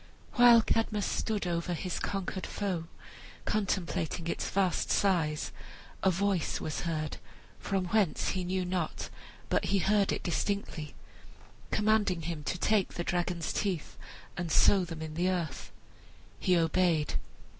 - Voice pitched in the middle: Yes, medium, 180 Hz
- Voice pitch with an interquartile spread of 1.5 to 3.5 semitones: Yes, average, 2.9 semitones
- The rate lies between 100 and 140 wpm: Yes, slow, 135 wpm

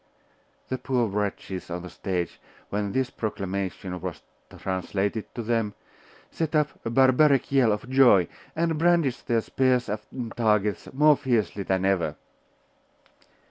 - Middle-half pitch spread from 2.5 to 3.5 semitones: No, average, 5.1 semitones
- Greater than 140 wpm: No, slow, 135 wpm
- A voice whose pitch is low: Yes, low, 110 Hz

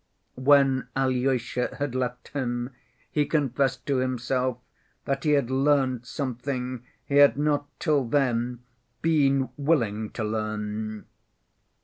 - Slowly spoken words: Yes, slow, 115 wpm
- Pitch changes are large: No, narrow, 2.6 semitones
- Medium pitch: No, low, 130 Hz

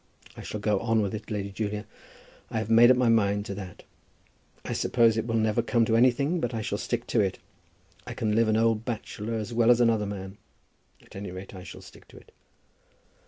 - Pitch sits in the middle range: No, low, 110 Hz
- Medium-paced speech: No, fast, 220 wpm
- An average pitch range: No, narrow, 2.1 semitones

